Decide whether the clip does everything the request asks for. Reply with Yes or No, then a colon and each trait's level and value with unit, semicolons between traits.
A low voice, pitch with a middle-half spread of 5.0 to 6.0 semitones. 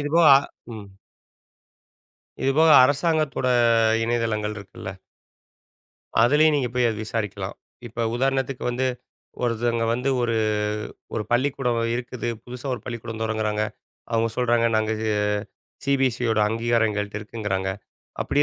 No: low, 120 Hz; average, 2.9 semitones